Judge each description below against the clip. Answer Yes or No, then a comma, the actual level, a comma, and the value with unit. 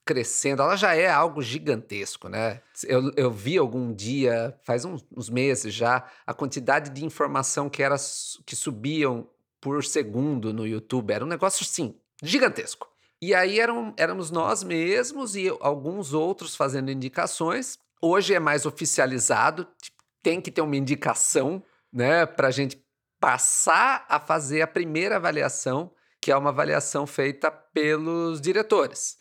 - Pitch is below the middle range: No, medium, 145 Hz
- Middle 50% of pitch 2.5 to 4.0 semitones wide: No, average, 4.4 semitones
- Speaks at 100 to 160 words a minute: Yes, average, 145 wpm